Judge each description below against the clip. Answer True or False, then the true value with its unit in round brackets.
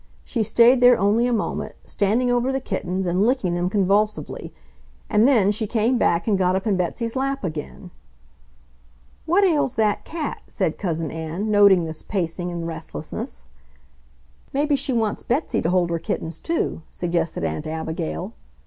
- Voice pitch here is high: True (205 Hz)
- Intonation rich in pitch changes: True (5.8 semitones)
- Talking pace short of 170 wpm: True (160 wpm)